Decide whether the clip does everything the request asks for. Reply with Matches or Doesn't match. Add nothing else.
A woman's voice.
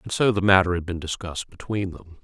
Doesn't match